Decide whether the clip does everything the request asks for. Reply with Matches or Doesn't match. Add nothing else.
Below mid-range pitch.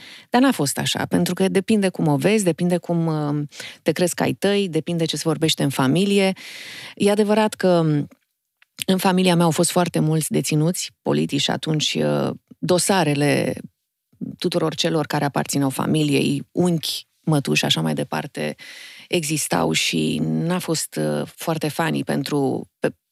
Doesn't match